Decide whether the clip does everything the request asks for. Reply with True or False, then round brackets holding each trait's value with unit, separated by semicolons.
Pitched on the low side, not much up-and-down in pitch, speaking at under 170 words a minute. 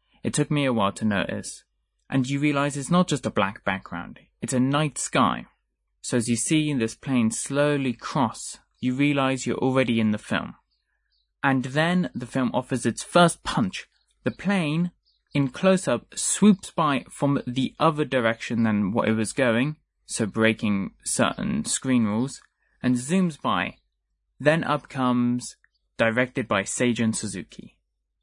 False (130 Hz; 4.0 semitones; 155 wpm)